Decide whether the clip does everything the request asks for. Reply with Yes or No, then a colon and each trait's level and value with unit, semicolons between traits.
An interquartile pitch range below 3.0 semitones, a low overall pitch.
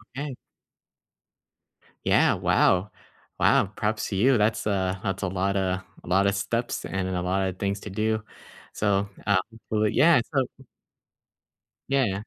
Yes: narrow, 2.4 semitones; low, 100 Hz